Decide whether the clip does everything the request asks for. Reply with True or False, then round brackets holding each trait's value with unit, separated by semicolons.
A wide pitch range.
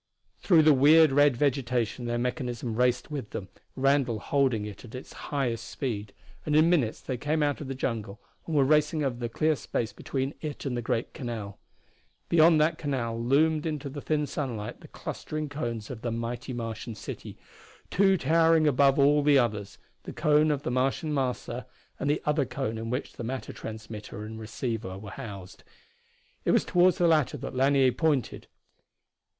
False (4.2 semitones)